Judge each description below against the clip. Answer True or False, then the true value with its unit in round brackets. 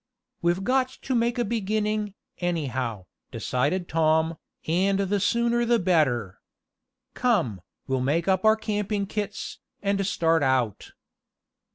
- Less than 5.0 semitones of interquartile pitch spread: False (5.5 semitones)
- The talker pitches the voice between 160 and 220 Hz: True (190 Hz)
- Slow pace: True (125 wpm)